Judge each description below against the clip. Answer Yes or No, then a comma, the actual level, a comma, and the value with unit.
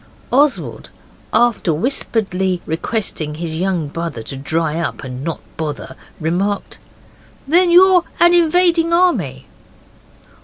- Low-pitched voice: No, medium, 185 Hz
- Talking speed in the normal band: No, slow, 110 wpm